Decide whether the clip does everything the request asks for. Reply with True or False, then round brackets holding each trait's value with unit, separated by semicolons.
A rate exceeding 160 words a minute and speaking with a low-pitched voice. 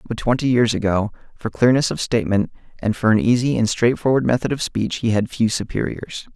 True (200 wpm; 115 Hz)